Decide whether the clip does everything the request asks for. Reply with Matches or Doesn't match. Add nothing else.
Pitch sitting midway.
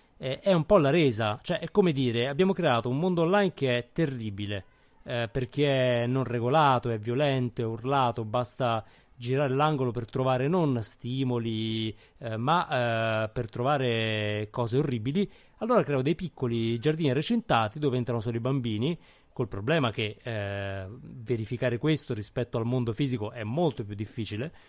Doesn't match